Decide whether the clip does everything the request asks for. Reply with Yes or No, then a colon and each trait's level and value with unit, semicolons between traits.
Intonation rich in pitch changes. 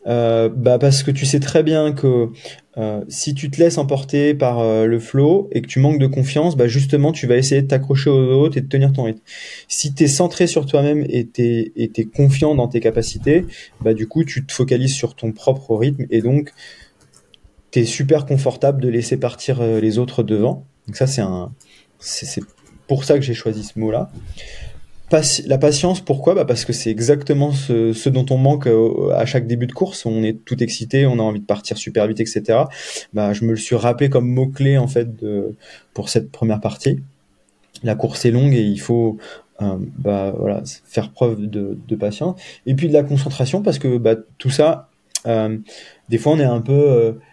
No: average, 3.9 semitones